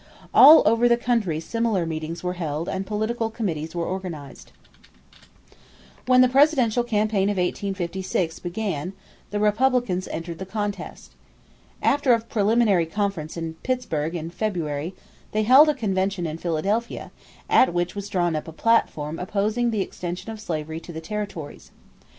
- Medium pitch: No, high, 195 Hz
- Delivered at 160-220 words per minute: No, average, 145 wpm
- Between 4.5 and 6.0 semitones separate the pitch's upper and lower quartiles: Yes, average, 4.9 semitones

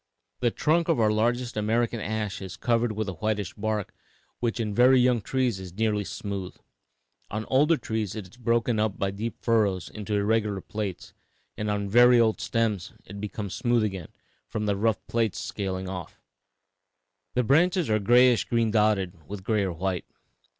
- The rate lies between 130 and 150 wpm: No, average, 170 wpm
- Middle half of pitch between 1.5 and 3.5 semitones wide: Yes, average, 2.8 semitones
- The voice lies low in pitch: Yes, low, 110 Hz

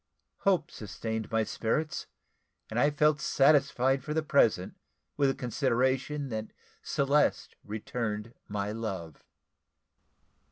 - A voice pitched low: Yes, low, 125 Hz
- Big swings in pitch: No, average, 4.8 semitones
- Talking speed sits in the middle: No, slow, 110 wpm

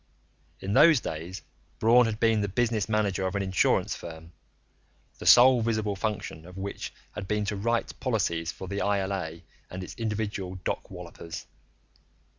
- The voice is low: Yes, low, 100 Hz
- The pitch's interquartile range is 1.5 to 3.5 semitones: Yes, average, 3.0 semitones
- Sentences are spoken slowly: No, average, 155 wpm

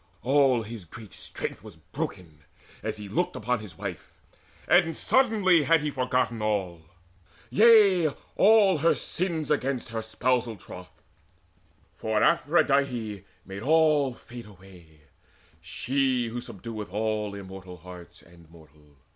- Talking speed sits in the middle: No, slow, 125 wpm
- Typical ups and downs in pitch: No, wide, 7.1 semitones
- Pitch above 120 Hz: No, low, 115 Hz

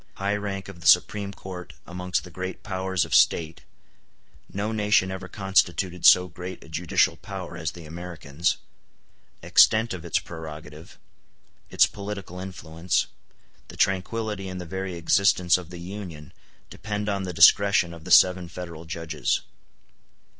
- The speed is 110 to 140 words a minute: Yes, slow, 135 wpm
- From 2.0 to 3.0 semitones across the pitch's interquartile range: Yes, narrow, 2.5 semitones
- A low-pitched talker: Yes, very low, 90 Hz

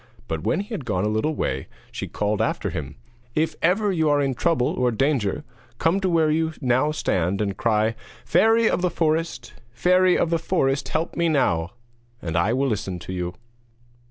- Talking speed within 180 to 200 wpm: Yes, average, 190 wpm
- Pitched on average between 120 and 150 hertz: Yes, low, 135 Hz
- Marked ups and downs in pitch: Yes, wide, 8.1 semitones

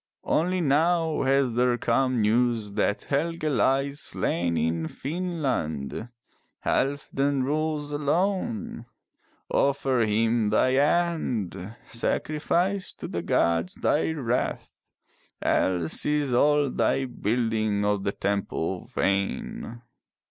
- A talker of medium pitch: No, low, 130 Hz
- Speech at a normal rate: No, slow, 100 wpm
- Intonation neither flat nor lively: No, wide, 6.1 semitones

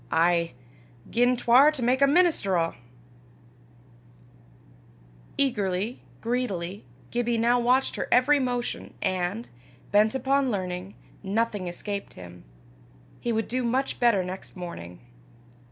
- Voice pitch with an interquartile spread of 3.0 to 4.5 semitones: No, average, 5.3 semitones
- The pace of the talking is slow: Yes, slow, 115 wpm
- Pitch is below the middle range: No, high, 230 Hz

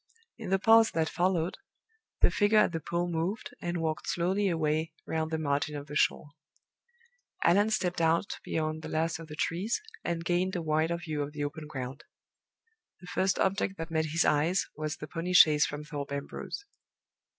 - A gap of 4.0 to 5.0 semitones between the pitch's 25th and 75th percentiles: No, average, 2.7 semitones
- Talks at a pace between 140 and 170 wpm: No, average, 185 wpm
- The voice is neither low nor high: Yes, medium, 165 Hz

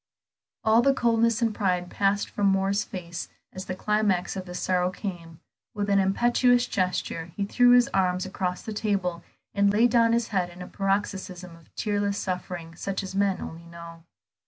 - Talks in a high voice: Yes, high, 195 Hz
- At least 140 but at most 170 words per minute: No, average, 180 wpm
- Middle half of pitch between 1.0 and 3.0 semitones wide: Yes, average, 2.7 semitones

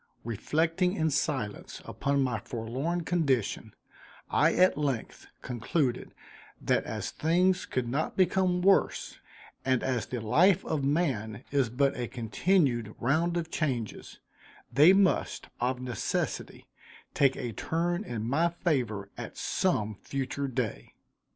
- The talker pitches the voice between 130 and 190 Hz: Yes, medium, 140 Hz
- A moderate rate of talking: No, slow, 125 wpm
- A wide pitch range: Yes, wide, 6.0 semitones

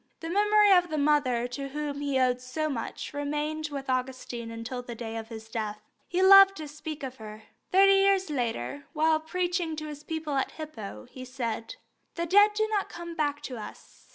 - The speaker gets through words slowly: No, average, 195 wpm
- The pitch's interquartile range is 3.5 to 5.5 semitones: Yes, average, 5.1 semitones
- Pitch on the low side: No, very high, 290 Hz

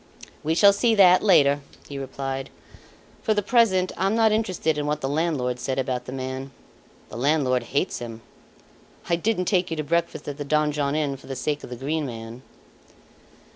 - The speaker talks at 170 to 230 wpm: Yes, average, 185 wpm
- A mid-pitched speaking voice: Yes, medium, 150 Hz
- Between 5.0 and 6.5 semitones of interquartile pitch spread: Yes, average, 5.3 semitones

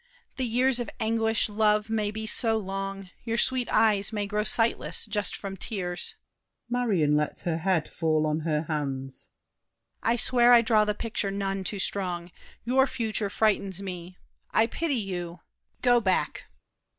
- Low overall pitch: No, high, 210 Hz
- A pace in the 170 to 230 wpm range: No, average, 160 wpm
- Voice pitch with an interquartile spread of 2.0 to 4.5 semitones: Yes, average, 3.9 semitones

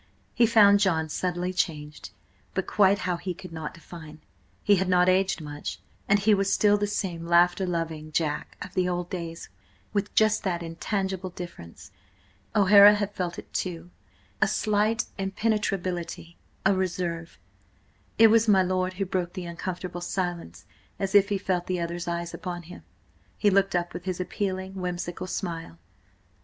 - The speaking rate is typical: Yes, average, 160 wpm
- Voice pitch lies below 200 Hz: Yes, medium, 185 Hz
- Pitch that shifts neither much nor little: No, narrow, 2.3 semitones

